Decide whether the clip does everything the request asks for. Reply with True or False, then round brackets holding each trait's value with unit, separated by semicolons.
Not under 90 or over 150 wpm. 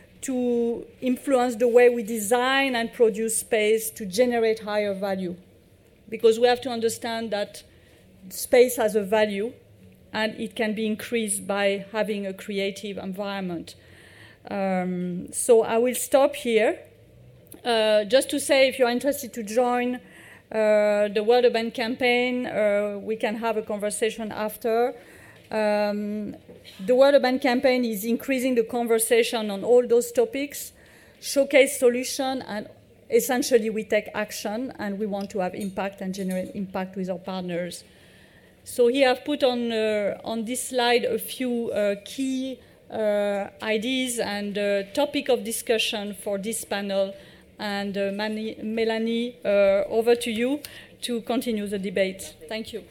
True (145 wpm)